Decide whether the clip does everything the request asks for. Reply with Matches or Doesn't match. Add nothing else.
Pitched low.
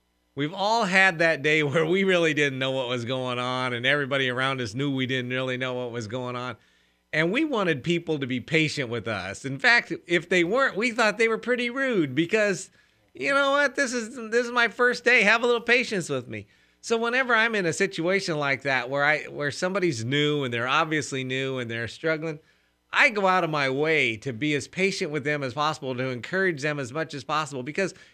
Doesn't match